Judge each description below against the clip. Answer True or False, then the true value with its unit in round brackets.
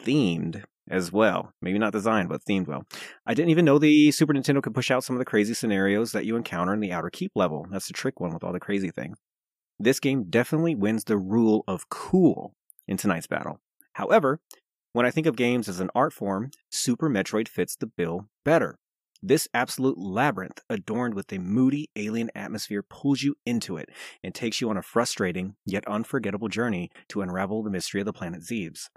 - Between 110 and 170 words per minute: False (205 wpm)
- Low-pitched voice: True (110 Hz)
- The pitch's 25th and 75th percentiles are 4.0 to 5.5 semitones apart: True (4.5 semitones)